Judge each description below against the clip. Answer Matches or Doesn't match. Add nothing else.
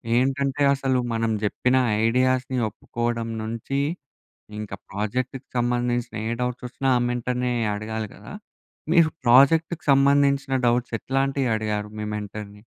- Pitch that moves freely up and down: Doesn't match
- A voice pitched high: Doesn't match